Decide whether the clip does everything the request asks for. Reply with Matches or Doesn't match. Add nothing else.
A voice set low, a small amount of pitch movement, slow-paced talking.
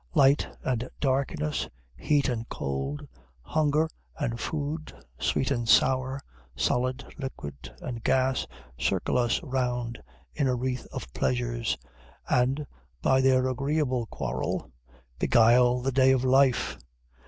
Matches